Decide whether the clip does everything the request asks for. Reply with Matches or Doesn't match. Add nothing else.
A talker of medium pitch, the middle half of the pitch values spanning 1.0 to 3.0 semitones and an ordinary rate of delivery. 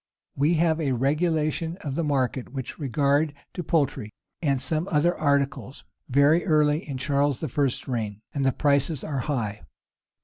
Matches